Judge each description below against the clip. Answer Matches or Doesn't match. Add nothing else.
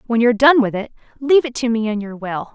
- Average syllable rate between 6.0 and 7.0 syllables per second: Matches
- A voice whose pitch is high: Matches